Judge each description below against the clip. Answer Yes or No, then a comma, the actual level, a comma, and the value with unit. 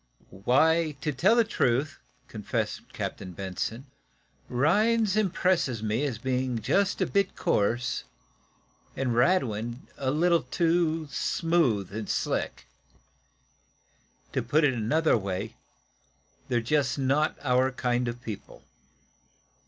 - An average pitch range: No, wide, 5.8 semitones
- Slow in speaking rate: Yes, slow, 115 wpm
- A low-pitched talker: Yes, low, 130 Hz